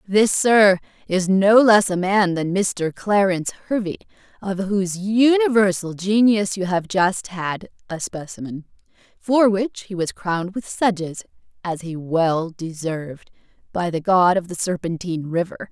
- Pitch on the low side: No, high, 190 Hz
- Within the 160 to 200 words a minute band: No, average, 150 wpm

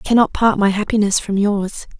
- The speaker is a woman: Yes, female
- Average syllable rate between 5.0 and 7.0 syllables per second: Yes, 5.6 syllables/s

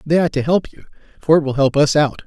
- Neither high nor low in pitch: Yes, medium, 150 Hz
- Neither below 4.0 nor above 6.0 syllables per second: No, 6.2 syllables/s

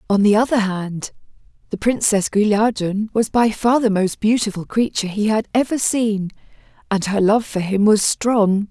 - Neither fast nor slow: Yes, average, 170 wpm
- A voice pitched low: No, high, 215 Hz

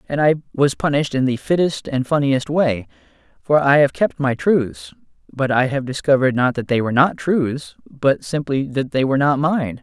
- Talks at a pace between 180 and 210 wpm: Yes, average, 200 wpm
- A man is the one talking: Yes, male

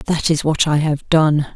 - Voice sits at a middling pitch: Yes, medium, 155 Hz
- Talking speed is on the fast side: Yes, fast, 230 wpm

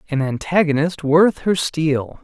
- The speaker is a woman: No, male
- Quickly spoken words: No, slow, 135 wpm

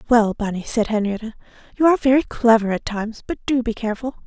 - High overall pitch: Yes, high, 230 Hz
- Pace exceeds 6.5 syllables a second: Yes, 6.8 syllables/s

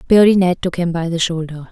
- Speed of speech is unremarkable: No, fast, 245 wpm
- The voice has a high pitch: No, medium, 175 Hz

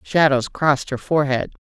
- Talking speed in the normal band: Yes, average, 150 wpm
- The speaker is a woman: Yes, female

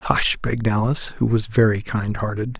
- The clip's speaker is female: No, male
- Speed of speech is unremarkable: Yes, average, 185 wpm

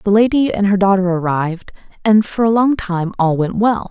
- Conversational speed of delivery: No, fast, 215 wpm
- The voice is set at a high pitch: Yes, high, 200 Hz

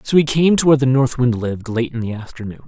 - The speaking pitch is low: Yes, low, 125 Hz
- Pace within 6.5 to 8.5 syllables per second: Yes, 6.8 syllables/s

